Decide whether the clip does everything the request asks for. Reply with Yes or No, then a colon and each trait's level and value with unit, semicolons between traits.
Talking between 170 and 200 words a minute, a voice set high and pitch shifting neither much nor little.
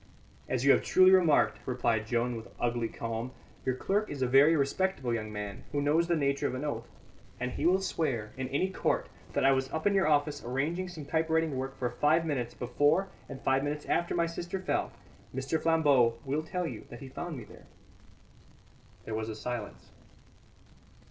No: average, 195 wpm; medium, 140 Hz; average, 4.8 semitones